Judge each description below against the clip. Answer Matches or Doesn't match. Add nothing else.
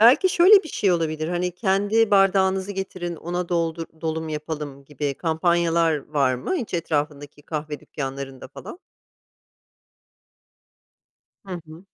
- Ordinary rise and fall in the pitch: Matches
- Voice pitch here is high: Doesn't match